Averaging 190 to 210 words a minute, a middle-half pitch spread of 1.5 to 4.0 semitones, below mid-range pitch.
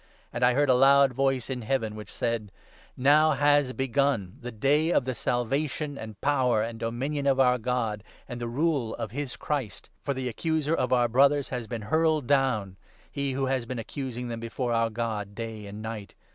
Yes: fast, 205 wpm; average, 3.4 semitones; low, 125 Hz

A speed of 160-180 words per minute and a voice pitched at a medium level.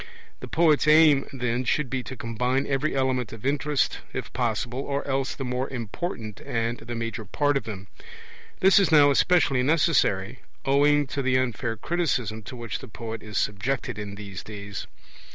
No: average, 170 wpm; low, 130 Hz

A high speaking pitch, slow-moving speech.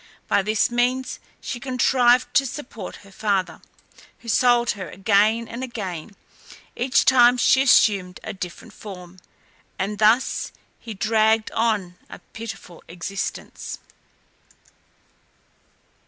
Yes: high, 220 Hz; slow, 110 wpm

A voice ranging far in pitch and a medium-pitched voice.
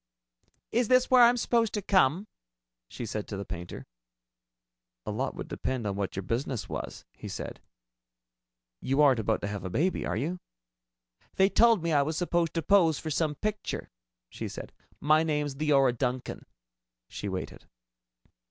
Yes: wide, 7.7 semitones; medium, 150 Hz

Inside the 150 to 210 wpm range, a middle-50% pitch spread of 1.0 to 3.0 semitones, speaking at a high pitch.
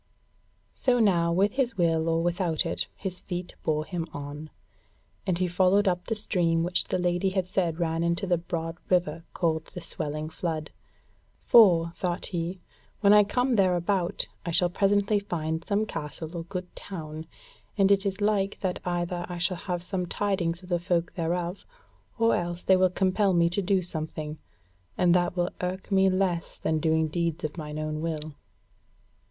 No: average, 175 wpm; narrow, 2.5 semitones; medium, 175 Hz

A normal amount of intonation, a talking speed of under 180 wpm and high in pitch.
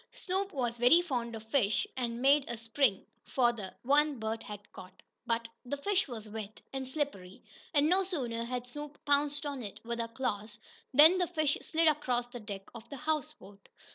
No: average, 4.6 semitones; average, 190 wpm; very high, 250 Hz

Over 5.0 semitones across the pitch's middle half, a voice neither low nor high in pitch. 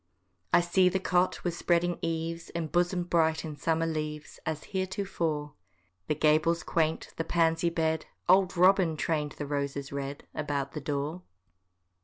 No: narrow, 2.4 semitones; medium, 165 Hz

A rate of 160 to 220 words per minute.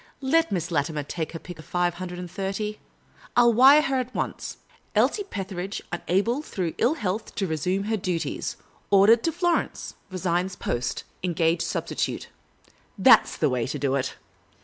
Yes: average, 185 wpm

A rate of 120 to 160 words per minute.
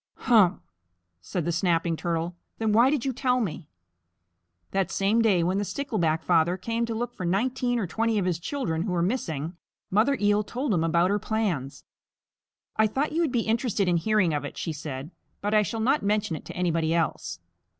No: average, 200 wpm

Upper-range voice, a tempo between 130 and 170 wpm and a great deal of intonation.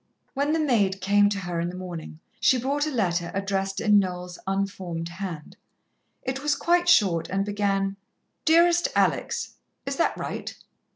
Yes: high, 195 Hz; average, 160 wpm; wide, 6.4 semitones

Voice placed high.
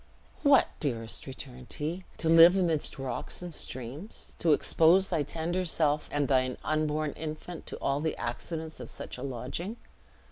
No: medium, 155 Hz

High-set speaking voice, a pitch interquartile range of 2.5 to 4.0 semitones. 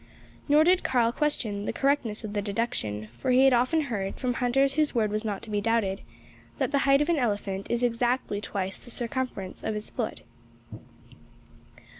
No: high, 235 Hz; average, 4.7 semitones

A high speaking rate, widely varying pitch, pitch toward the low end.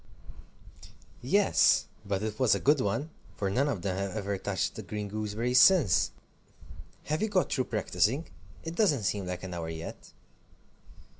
No: average, 160 wpm; wide, 6.0 semitones; low, 105 Hz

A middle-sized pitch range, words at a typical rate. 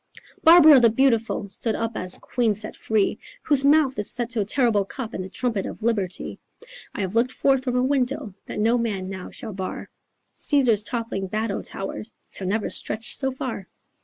Yes: average, 3.9 semitones; average, 190 wpm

